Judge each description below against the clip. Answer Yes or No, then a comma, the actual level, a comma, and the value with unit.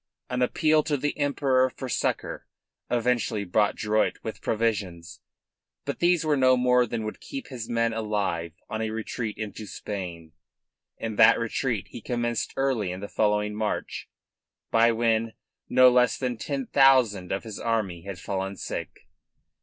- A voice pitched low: Yes, low, 115 Hz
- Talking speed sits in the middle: Yes, average, 155 wpm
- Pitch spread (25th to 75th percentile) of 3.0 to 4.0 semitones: Yes, average, 3.3 semitones